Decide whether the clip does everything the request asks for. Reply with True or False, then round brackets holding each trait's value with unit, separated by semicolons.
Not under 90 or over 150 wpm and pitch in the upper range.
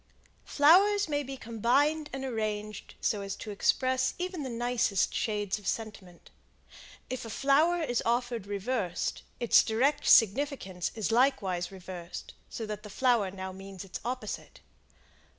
True (140 wpm; 230 Hz)